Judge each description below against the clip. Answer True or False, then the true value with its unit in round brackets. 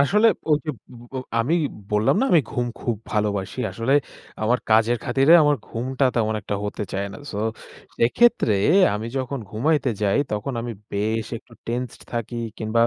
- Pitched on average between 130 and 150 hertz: False (120 Hz)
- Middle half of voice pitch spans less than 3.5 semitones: False (3.8 semitones)